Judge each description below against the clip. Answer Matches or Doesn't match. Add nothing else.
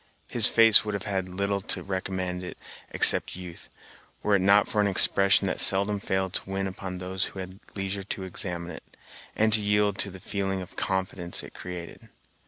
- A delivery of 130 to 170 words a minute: Doesn't match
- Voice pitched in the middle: Doesn't match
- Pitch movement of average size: Doesn't match